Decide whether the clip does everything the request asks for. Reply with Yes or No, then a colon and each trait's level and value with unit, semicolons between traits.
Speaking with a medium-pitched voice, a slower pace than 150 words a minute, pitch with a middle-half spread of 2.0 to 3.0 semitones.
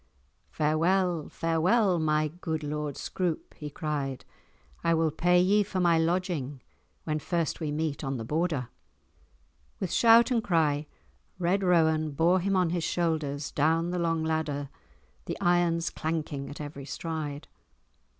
Yes: medium, 160 Hz; average, 140 wpm; average, 2.7 semitones